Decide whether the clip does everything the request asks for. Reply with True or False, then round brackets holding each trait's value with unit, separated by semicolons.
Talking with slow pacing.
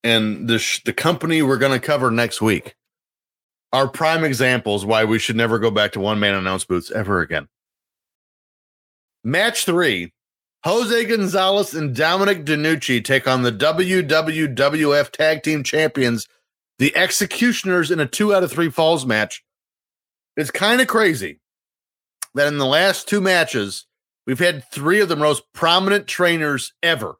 False (150 wpm)